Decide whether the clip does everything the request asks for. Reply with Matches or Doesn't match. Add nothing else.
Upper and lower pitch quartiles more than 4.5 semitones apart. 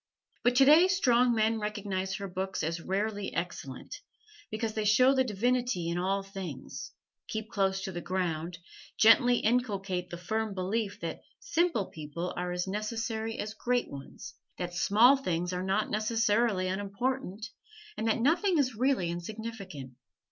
Doesn't match